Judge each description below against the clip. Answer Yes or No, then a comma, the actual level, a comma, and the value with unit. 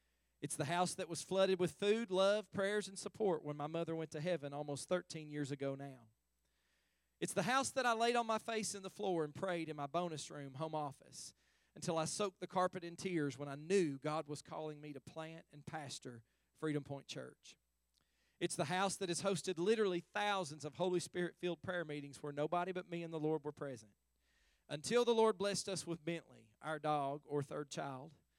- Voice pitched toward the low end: No, medium, 160 Hz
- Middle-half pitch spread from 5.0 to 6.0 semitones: No, average, 4.4 semitones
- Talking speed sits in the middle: No, fast, 210 wpm